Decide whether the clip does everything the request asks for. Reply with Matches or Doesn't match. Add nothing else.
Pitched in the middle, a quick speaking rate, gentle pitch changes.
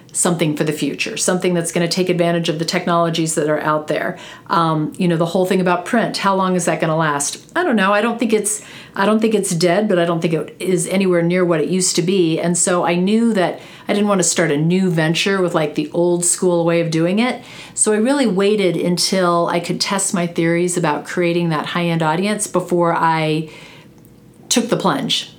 Matches